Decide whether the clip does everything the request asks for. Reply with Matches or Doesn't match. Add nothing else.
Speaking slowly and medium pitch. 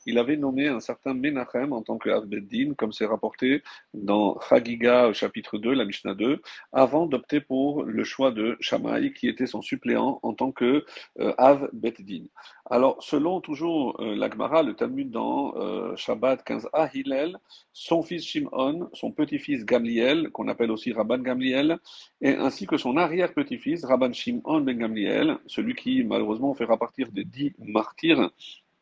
Doesn't match